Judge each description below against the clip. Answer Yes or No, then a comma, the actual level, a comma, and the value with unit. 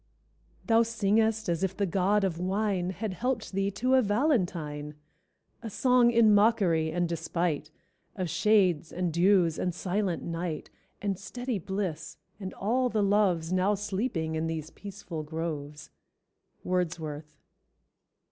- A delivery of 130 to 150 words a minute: Yes, average, 140 wpm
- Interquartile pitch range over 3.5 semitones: Yes, average, 4.2 semitones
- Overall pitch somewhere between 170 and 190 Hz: Yes, medium, 185 Hz